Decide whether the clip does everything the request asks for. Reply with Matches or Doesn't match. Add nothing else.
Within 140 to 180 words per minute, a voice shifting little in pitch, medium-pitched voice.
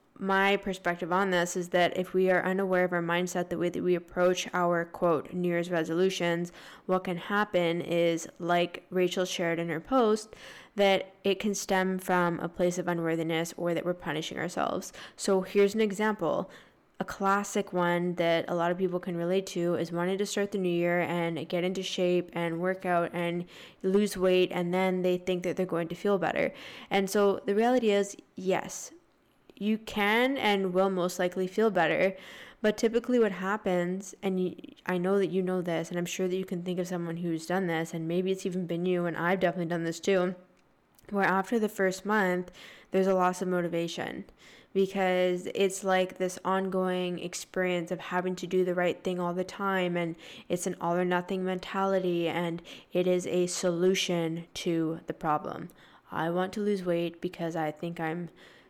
Doesn't match